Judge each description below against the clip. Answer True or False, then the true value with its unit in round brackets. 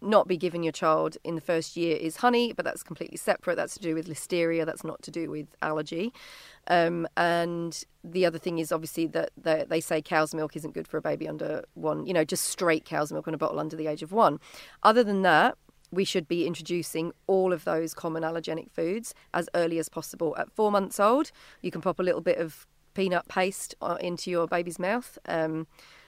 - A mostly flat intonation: True (2.2 semitones)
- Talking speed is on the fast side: True (215 wpm)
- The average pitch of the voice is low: False (170 Hz)